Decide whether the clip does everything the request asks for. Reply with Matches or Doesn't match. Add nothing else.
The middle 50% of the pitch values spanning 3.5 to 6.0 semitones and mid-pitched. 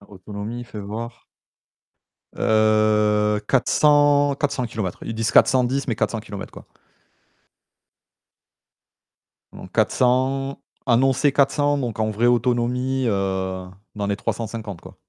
Doesn't match